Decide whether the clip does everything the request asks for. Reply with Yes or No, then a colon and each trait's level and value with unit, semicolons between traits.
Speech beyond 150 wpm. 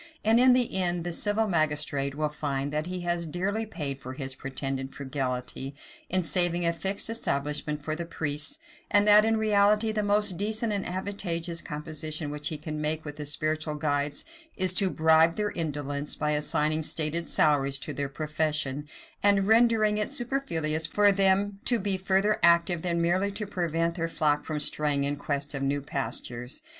Yes: average, 175 wpm